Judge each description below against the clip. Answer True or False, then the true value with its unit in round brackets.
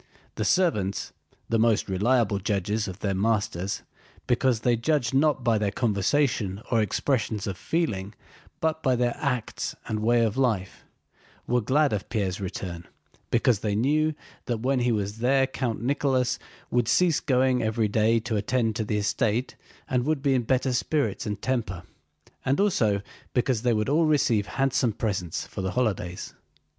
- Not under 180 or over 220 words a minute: False (160 wpm)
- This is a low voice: True (115 Hz)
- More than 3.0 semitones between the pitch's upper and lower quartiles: True (4.0 semitones)